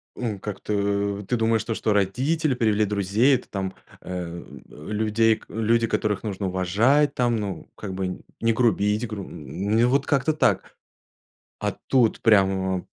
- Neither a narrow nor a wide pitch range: Yes, average, 3.2 semitones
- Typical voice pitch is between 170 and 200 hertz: No, low, 105 Hz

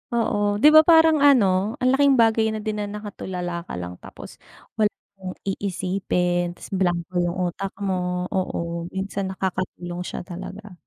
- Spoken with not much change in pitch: No, average, 3.0 semitones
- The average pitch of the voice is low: No, high, 190 Hz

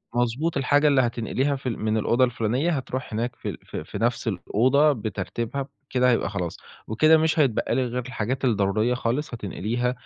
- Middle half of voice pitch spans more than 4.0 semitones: No, average, 3.4 semitones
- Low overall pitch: Yes, low, 125 Hz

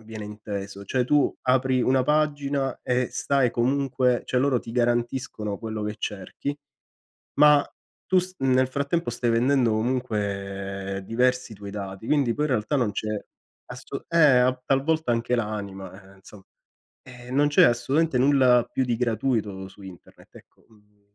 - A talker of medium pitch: No, low, 125 Hz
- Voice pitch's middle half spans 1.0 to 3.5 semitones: No, average, 4.2 semitones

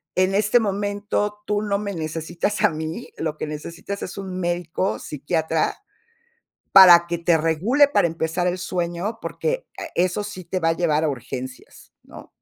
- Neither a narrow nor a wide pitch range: Yes, average, 3.9 semitones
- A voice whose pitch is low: No, medium, 175 Hz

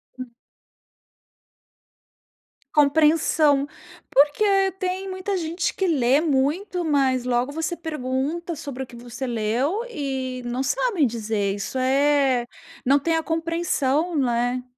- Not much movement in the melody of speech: No, average, 4.4 semitones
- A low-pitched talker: No, very high, 280 Hz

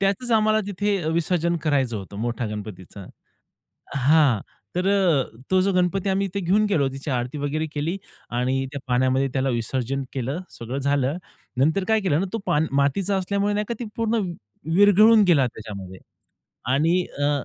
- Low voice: No, medium, 155 Hz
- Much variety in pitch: Yes, wide, 7.0 semitones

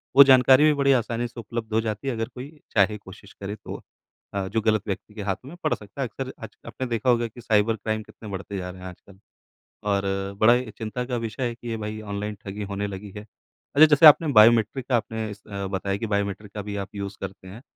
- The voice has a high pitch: No, low, 110 Hz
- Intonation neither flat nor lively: Yes, average, 3.1 semitones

